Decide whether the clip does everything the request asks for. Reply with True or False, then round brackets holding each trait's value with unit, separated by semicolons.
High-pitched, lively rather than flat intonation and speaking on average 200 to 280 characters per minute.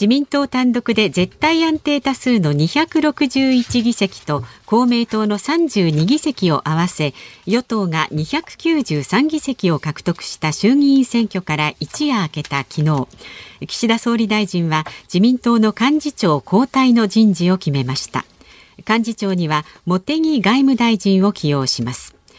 True (210 Hz; 8.7 semitones; 245 characters per minute)